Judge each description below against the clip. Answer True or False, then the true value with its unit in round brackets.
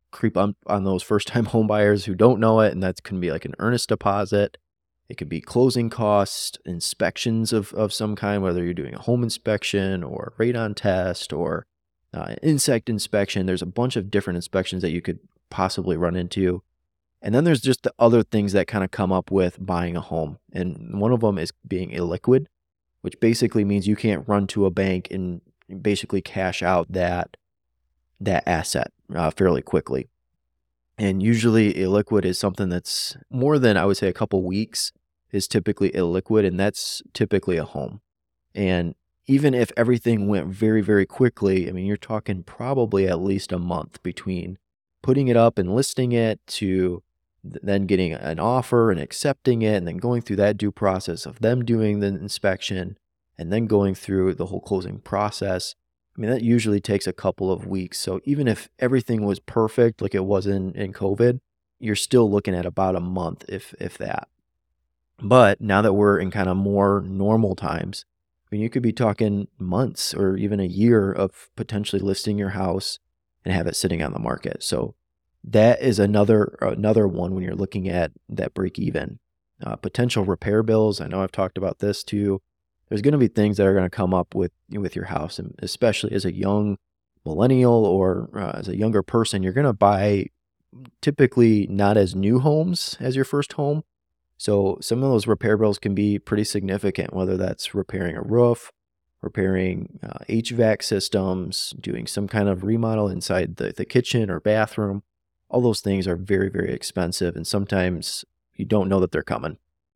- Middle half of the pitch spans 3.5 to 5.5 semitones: False (3.1 semitones)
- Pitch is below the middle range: True (100 Hz)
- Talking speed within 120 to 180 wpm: False (190 wpm)